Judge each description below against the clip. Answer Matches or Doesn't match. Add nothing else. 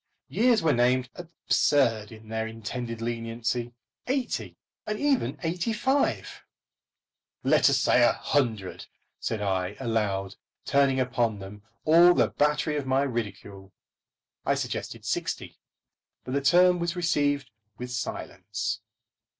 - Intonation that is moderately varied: Doesn't match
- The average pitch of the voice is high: Doesn't match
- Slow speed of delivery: Matches